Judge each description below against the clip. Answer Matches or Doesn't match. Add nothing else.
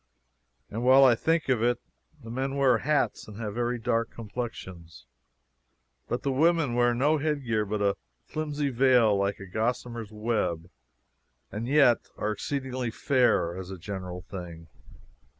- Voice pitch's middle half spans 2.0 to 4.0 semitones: Doesn't match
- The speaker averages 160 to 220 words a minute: Doesn't match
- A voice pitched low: Matches